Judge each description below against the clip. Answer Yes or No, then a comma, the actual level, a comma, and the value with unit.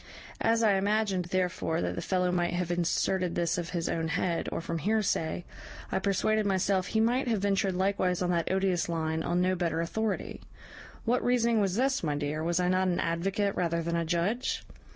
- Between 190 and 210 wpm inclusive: Yes, average, 195 wpm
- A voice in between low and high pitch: Yes, medium, 180 Hz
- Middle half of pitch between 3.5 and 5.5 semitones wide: No, average, 3.1 semitones